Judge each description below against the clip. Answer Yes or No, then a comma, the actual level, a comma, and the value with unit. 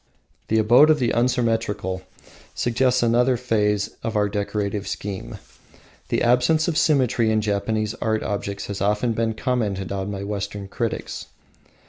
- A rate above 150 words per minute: No, average, 140 wpm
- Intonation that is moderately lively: Yes, average, 3.1 semitones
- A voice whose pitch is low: Yes, low, 110 Hz